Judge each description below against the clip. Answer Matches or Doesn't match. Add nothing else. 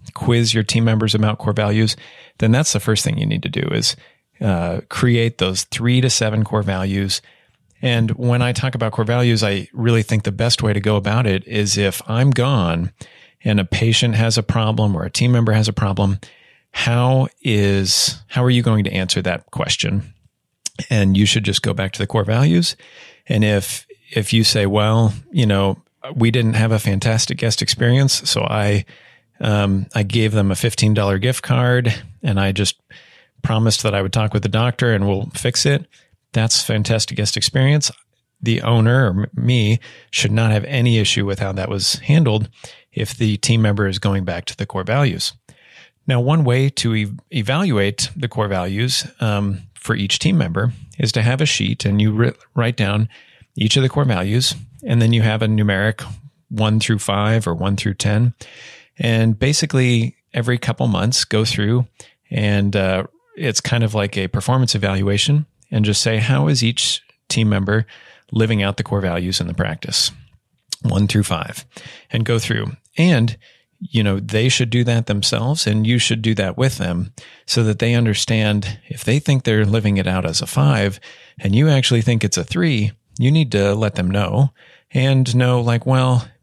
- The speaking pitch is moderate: Doesn't match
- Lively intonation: Doesn't match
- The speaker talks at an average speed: Matches